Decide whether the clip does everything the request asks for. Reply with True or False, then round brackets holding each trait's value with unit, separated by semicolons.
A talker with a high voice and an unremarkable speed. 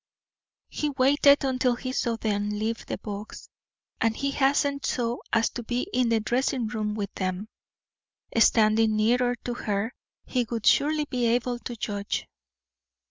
True (235 Hz; 150 wpm)